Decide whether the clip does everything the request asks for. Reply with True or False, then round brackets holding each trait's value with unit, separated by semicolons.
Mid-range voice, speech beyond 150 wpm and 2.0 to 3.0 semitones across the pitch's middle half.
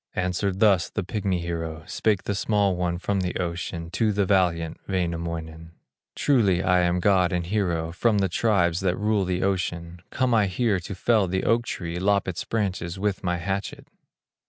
False (90 Hz; 180 wpm; 2.7 semitones)